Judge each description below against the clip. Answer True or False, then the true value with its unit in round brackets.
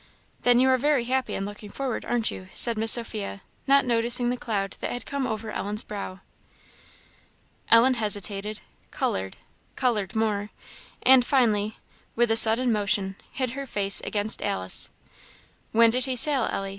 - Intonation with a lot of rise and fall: False (3.4 semitones)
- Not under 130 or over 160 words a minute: True (155 wpm)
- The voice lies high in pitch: True (225 Hz)